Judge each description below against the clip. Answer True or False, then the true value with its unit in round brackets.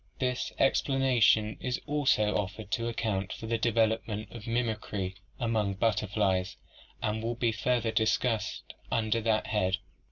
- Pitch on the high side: False (110 Hz)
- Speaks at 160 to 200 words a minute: False (140 wpm)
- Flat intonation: True (1.9 semitones)